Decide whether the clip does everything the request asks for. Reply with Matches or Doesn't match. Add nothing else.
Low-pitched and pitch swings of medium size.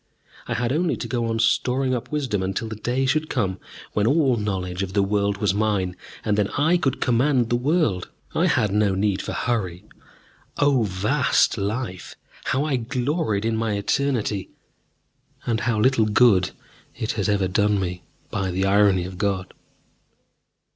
Matches